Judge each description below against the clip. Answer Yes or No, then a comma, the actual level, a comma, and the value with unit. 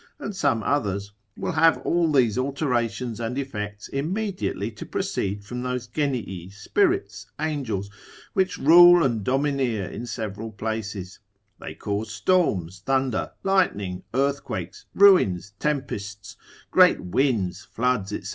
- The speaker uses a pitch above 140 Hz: No, low, 120 Hz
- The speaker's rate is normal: No, slow, 120 wpm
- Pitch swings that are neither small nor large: No, wide, 6.0 semitones